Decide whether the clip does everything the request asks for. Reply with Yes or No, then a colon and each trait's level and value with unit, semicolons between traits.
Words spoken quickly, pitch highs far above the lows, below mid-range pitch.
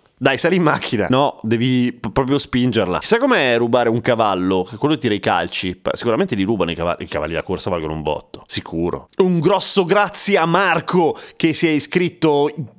Yes: fast, 190 wpm; wide, 8.2 semitones; low, 125 Hz